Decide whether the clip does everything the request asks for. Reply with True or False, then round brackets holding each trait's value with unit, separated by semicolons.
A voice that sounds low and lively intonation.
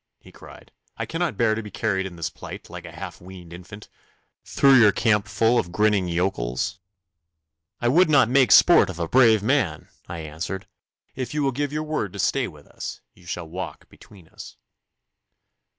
True (100 Hz; 6.2 semitones)